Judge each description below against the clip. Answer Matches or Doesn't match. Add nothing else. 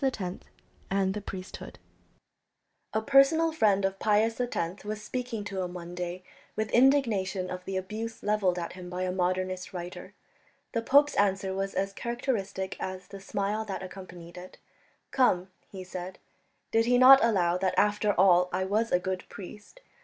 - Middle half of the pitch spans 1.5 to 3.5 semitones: Matches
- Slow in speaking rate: Doesn't match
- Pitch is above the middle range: Matches